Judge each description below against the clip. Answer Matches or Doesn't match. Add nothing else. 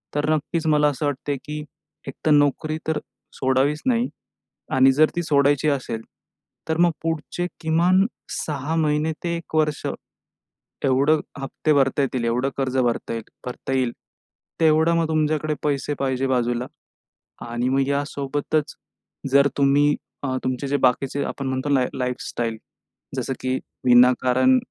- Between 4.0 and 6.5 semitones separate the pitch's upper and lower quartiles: Doesn't match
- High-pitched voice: Doesn't match